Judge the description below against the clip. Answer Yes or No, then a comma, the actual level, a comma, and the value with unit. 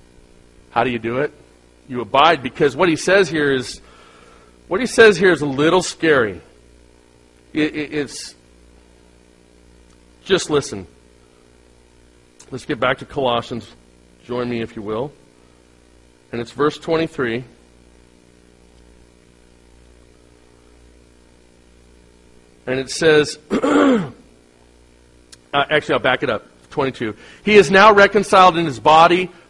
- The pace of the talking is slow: Yes, slow, 115 wpm